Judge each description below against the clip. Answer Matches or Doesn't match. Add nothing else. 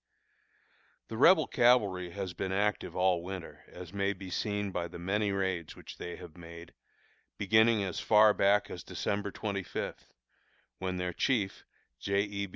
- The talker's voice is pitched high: Doesn't match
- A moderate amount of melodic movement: Doesn't match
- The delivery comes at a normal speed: Matches